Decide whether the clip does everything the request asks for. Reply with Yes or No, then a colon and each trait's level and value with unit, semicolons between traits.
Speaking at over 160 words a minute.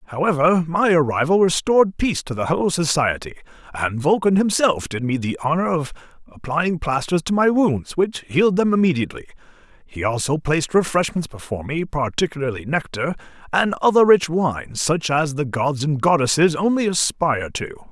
No: average, 155 wpm